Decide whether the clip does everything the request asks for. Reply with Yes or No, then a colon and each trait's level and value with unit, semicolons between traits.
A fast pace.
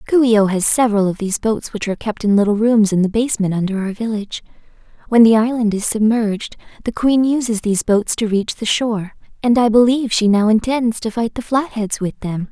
Yes: fast, 220 wpm